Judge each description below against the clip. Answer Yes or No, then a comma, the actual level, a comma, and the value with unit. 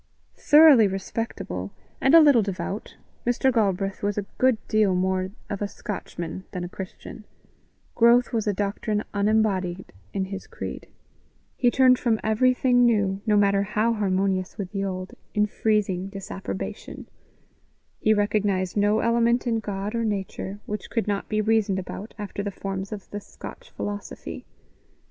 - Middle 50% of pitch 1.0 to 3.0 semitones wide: Yes, narrow, 2.6 semitones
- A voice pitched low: No, high, 205 Hz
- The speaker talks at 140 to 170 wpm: Yes, average, 150 wpm